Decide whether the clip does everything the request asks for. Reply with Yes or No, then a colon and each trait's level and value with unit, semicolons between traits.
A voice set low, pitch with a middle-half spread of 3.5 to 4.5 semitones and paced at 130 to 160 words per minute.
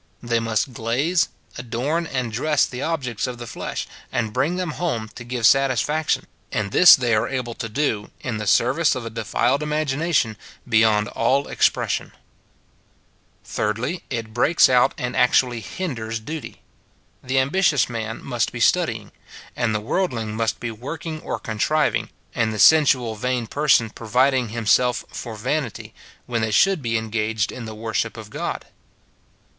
Yes: low, 120 Hz; average, 4.0 semitones; average, 155 wpm